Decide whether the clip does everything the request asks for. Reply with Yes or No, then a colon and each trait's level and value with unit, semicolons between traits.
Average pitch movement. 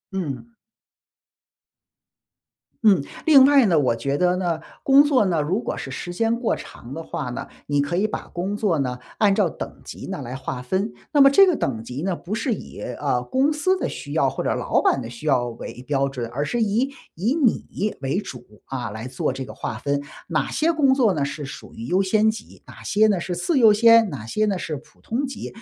No: wide, 8.9 semitones